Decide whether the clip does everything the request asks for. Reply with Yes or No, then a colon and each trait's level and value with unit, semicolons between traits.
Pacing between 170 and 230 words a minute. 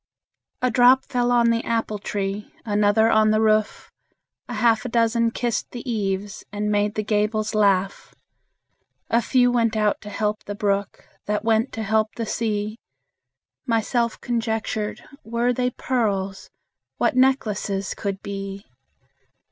No: average, 140 wpm